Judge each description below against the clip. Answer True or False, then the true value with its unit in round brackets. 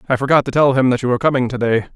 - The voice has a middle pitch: False (130 Hz)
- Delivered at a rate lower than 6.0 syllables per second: False (8.5 syllables/s)